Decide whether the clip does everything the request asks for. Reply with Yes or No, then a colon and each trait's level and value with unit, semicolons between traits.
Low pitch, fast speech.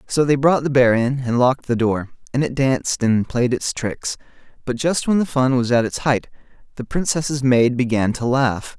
Yes: low, 130 Hz; fast, 220 wpm